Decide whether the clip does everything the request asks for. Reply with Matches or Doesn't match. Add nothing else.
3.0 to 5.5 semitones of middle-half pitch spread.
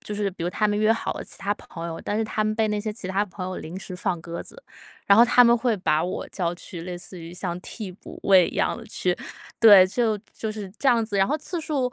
Matches